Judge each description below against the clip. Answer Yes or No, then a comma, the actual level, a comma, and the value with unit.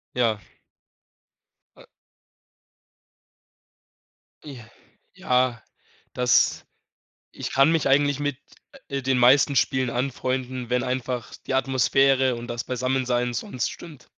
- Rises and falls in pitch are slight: Yes, narrow, 1.7 semitones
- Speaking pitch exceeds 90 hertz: Yes, low, 130 Hz